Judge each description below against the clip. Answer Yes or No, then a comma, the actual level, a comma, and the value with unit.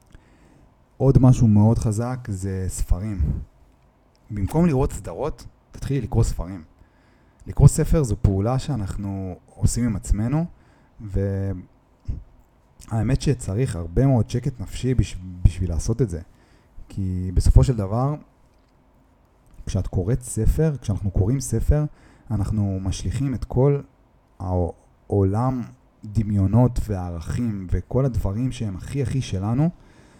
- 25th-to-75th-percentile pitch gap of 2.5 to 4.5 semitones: No, average, 5.1 semitones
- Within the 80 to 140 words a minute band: Yes, average, 105 wpm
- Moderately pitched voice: No, low, 105 Hz